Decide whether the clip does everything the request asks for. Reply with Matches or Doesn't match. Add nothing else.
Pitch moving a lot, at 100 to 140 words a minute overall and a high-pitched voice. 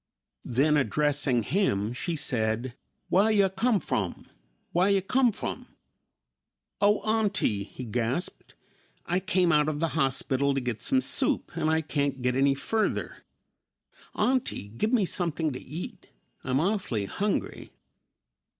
Doesn't match